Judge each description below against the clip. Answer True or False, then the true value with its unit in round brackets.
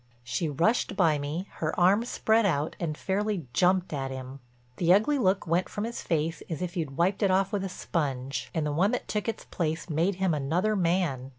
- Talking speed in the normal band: False (210 wpm)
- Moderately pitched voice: True (175 Hz)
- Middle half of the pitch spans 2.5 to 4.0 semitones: False (4.4 semitones)